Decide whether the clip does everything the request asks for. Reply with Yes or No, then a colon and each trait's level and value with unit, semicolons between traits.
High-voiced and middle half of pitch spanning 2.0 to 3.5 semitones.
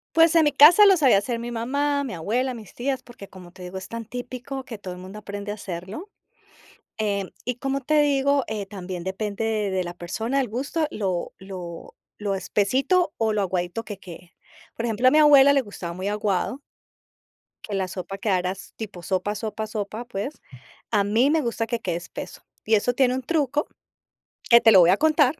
No: high, 220 Hz; wide, 5.5 semitones